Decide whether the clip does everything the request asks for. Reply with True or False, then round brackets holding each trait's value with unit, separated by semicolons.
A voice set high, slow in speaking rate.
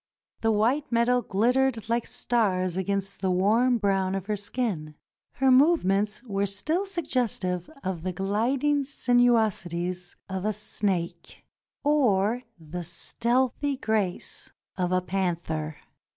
True (205 Hz; 120 wpm)